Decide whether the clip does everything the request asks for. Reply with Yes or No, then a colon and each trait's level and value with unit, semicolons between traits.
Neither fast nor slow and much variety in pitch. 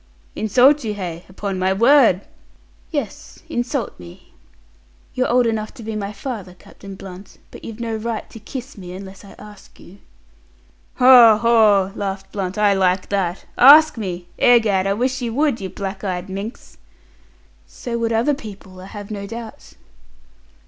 No: average, 160 wpm; average, 3.4 semitones